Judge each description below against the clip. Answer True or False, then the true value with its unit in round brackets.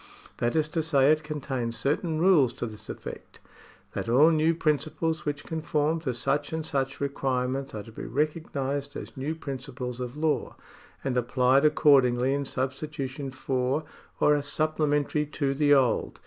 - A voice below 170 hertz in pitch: True (140 Hz)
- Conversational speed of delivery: True (160 wpm)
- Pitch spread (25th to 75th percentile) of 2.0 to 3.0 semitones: True (2.6 semitones)